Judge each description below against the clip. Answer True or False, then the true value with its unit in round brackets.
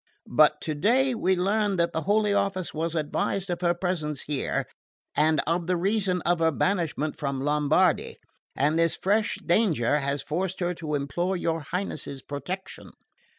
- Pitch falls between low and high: True (170 Hz)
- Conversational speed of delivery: True (155 wpm)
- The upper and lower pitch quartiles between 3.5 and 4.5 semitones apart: True (4.0 semitones)